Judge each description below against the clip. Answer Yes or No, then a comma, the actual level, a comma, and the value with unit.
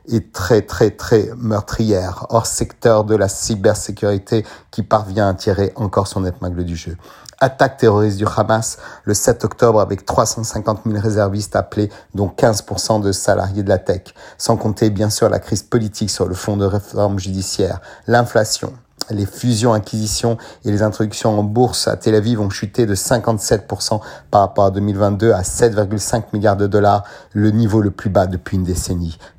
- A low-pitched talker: Yes, low, 105 Hz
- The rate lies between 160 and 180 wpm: Yes, average, 170 wpm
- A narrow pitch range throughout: Yes, narrow, 2.2 semitones